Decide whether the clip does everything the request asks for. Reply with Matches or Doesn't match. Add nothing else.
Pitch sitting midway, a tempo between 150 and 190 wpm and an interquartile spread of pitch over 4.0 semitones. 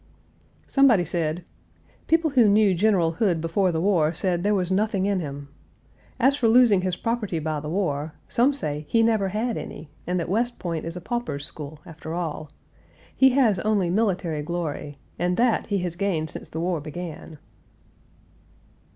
Matches